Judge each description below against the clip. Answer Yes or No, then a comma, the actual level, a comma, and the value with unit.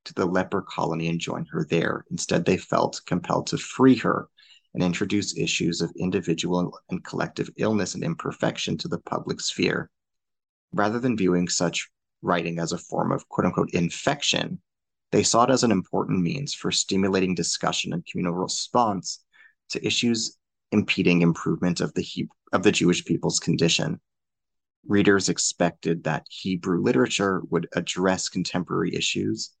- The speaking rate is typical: Yes, average, 150 wpm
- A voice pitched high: No, very low, 90 Hz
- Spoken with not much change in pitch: No, average, 3.1 semitones